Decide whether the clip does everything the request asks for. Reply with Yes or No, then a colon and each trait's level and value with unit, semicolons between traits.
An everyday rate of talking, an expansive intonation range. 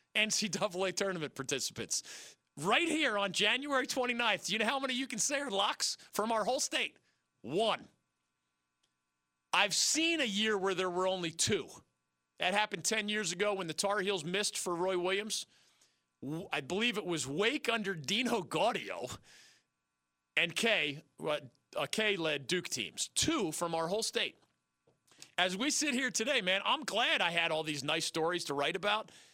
Yes: average, 165 wpm; wide, 6.8 semitones